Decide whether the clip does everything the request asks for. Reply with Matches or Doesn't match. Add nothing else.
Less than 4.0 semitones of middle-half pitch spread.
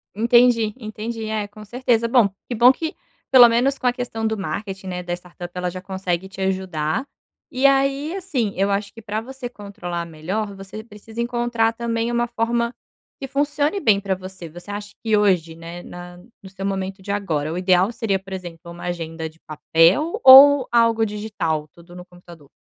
Doesn't match